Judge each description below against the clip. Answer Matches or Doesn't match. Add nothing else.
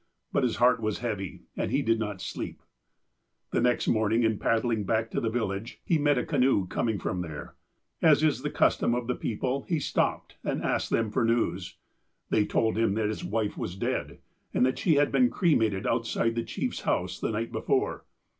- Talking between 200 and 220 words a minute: Matches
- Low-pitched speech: Matches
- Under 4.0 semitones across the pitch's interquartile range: Matches